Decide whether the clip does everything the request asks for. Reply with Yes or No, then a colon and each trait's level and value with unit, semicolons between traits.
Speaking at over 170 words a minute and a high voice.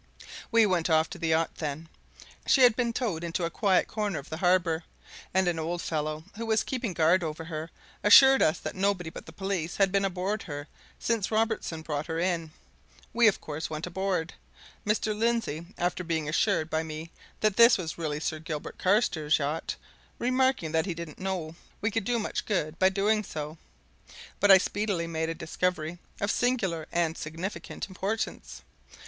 No: average, 180 wpm; medium, 175 Hz